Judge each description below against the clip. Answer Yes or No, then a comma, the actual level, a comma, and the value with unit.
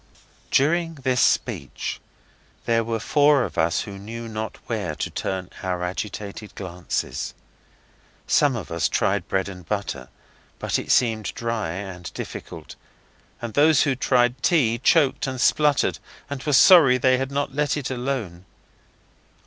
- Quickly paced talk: No, average, 145 wpm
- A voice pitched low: Yes, low, 115 Hz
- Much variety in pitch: Yes, wide, 6.0 semitones